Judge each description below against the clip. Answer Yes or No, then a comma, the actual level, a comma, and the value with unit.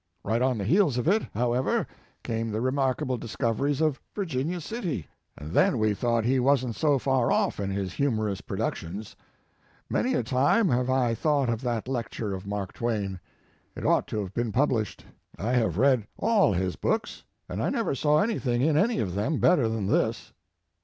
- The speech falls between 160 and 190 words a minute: Yes, average, 185 wpm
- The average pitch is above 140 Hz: No, low, 120 Hz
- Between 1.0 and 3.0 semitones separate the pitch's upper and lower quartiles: No, average, 4.7 semitones